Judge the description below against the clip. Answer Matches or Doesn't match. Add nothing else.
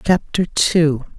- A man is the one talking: Doesn't match